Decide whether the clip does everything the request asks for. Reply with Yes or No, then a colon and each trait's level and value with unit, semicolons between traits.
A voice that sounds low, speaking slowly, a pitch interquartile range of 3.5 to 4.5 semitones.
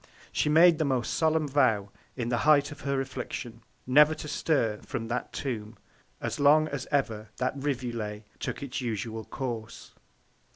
No: low, 130 Hz; average, 160 wpm; average, 4.2 semitones